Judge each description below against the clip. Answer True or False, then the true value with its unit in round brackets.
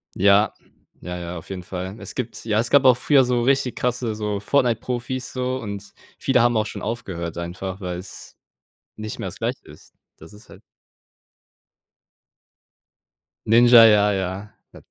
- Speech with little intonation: False (4.2 semitones)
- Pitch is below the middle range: True (110 Hz)